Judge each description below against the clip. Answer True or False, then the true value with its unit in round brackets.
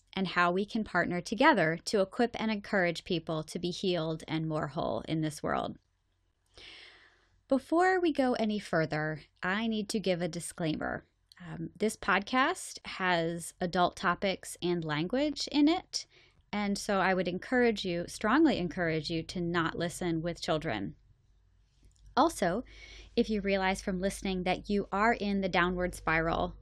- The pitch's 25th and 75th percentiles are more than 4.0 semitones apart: True (4.4 semitones)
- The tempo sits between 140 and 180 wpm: True (155 wpm)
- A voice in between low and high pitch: True (180 Hz)